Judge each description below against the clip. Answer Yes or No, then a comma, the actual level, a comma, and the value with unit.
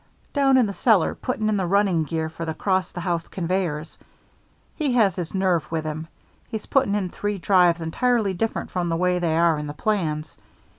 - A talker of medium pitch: Yes, medium, 180 Hz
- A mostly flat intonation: No, average, 4.0 semitones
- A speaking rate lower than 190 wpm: No, average, 200 wpm